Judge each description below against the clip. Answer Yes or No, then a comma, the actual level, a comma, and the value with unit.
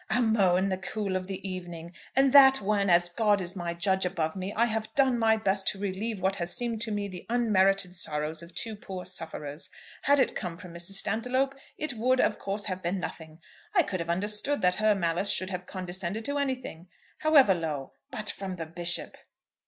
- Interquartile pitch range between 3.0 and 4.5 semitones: Yes, average, 4.0 semitones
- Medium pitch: No, high, 195 Hz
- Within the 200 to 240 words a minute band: Yes, fast, 205 wpm